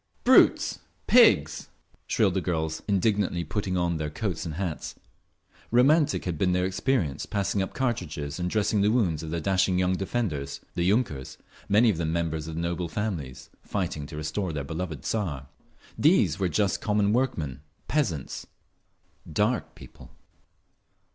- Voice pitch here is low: Yes, very low, 90 Hz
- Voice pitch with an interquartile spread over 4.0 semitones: Yes, average, 4.7 semitones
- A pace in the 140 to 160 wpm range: Yes, average, 150 wpm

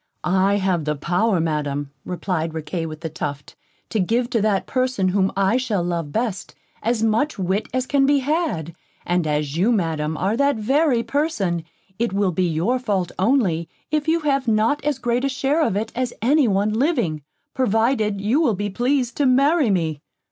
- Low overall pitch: No, high, 210 Hz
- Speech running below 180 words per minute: No, average, 185 wpm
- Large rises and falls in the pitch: Yes, wide, 6.7 semitones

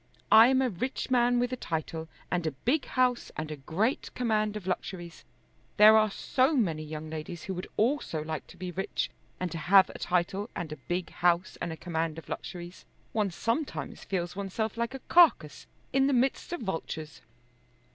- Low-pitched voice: No, high, 190 Hz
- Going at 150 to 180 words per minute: No, average, 190 wpm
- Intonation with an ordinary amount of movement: No, wide, 6.4 semitones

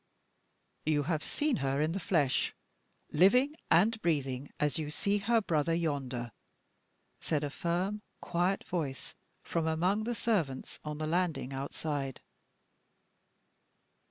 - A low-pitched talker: No, medium, 160 Hz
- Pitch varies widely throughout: No, average, 4.9 semitones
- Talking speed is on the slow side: Yes, slow, 125 wpm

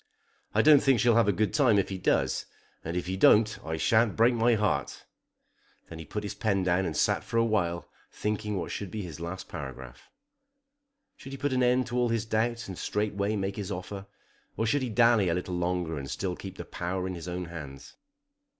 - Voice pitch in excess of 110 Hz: No, low, 100 Hz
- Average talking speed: No, fast, 220 wpm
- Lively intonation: No, average, 4.4 semitones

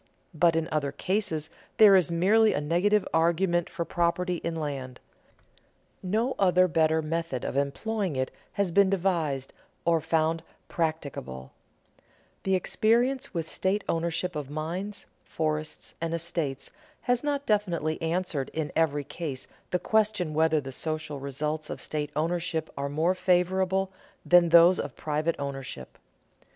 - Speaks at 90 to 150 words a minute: Yes, average, 140 wpm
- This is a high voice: No, medium, 165 Hz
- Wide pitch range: No, average, 3.3 semitones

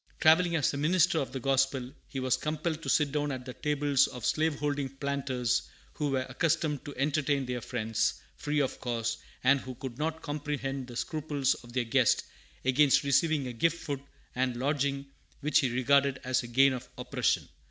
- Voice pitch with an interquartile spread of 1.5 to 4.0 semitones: Yes, narrow, 2.5 semitones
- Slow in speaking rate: No, average, 185 wpm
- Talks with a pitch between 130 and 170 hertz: Yes, medium, 140 Hz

